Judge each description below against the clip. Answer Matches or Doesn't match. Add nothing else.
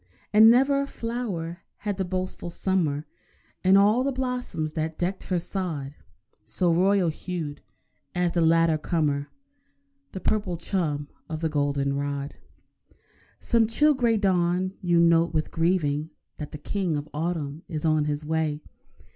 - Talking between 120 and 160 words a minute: Matches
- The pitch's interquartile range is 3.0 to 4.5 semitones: Matches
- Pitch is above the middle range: Doesn't match